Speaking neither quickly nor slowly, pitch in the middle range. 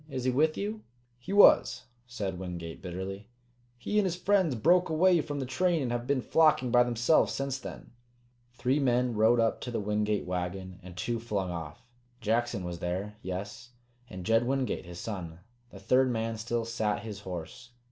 No: average, 180 wpm; low, 115 Hz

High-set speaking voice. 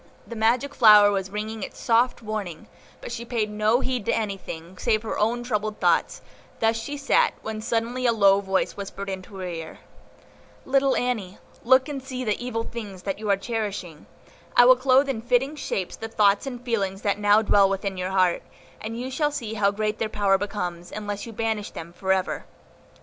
Yes: high, 215 Hz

